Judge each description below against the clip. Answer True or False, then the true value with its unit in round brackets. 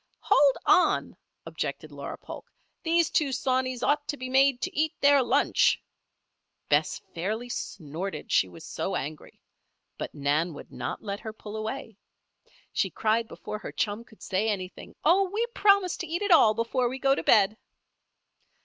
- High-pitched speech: True (235 Hz)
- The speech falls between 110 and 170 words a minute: True (165 wpm)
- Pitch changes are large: True (5.9 semitones)